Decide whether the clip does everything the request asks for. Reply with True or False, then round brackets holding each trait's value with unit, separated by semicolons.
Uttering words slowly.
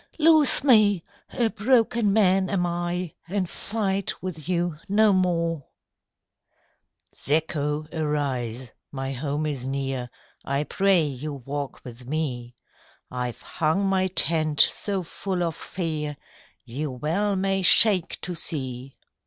True (120 wpm)